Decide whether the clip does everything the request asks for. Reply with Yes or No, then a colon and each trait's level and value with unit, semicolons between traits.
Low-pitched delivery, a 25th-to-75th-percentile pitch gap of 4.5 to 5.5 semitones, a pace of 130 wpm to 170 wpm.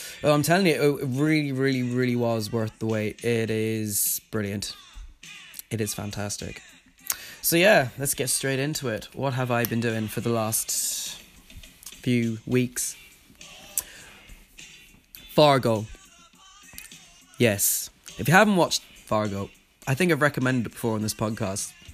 No: low, 115 Hz; average, 3.8 semitones; average, 140 wpm